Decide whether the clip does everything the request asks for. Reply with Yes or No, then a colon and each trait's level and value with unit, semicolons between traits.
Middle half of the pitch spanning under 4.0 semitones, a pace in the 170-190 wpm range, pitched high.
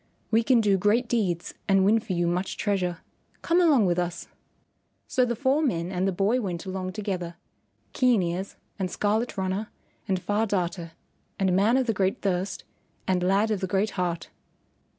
Yes: average, 3.5 semitones; average, 180 wpm; high, 195 Hz